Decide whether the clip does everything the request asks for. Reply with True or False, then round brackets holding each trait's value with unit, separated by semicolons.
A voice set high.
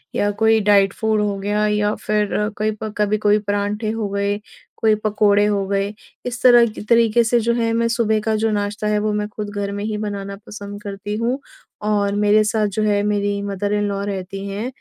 True (210 Hz)